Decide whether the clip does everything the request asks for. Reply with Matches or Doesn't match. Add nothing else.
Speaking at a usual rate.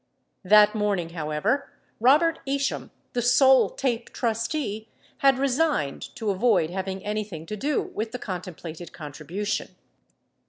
Doesn't match